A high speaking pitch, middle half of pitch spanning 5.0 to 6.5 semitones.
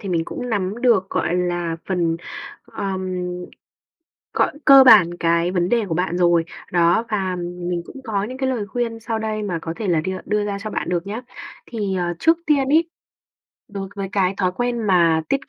No: high, 195 Hz; average, 4.3 semitones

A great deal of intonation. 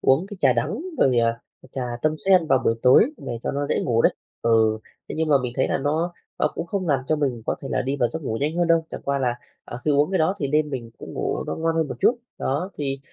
No: average, 4.2 semitones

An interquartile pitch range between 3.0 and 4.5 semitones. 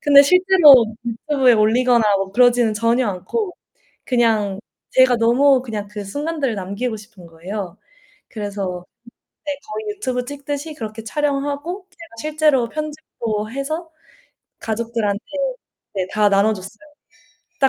No: average, 5.3 semitones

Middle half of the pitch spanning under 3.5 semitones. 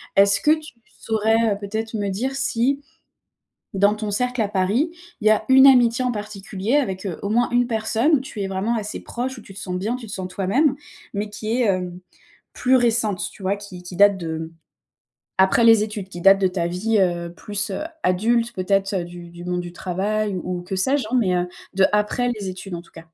No: average, 3.8 semitones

